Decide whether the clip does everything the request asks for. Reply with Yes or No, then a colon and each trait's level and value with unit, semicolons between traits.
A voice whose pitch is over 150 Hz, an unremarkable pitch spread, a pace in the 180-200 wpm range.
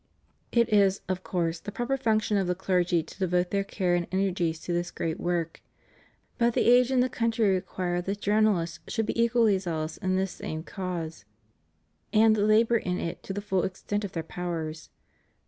Yes: high, 190 Hz; average, 3.6 semitones; average, 185 wpm